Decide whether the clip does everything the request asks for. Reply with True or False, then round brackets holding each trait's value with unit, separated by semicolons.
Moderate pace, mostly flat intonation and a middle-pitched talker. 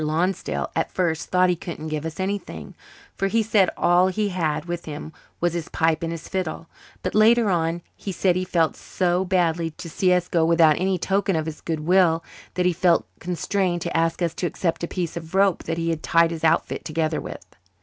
False (215 wpm; 2.1 semitones; 175 Hz)